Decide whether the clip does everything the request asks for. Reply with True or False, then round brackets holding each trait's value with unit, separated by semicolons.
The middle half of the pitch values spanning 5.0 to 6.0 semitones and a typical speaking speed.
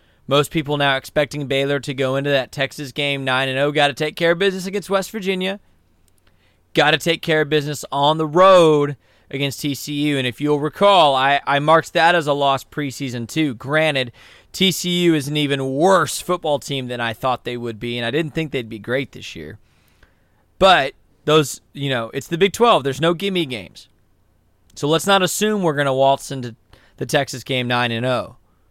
False (4.4 semitones; 190 wpm)